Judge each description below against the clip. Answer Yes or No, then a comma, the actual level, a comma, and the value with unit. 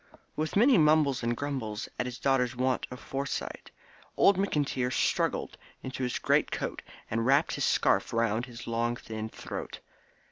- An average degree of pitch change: Yes, average, 3.4 semitones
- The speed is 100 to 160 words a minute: Yes, average, 155 wpm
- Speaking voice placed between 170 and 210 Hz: No, low, 125 Hz